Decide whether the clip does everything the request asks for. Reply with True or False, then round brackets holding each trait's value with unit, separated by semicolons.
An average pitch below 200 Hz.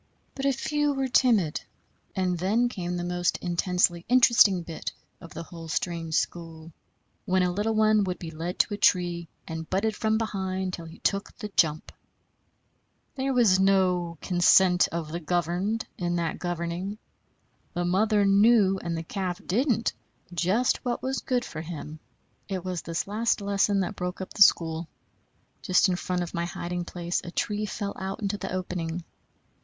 True (185 Hz)